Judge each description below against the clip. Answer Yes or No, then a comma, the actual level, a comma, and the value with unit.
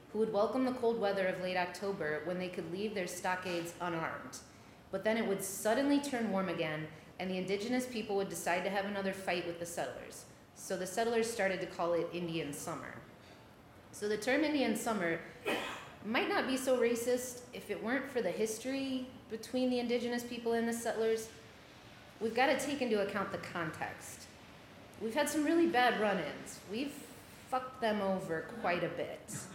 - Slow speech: No, average, 185 wpm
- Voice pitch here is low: No, high, 210 Hz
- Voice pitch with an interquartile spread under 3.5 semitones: No, average, 5.0 semitones